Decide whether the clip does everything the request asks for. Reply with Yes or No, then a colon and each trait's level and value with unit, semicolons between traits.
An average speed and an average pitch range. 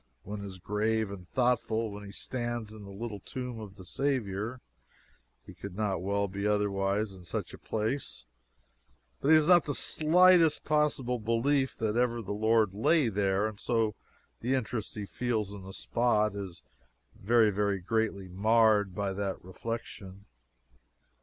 Yes: average, 160 wpm; average, 3.1 semitones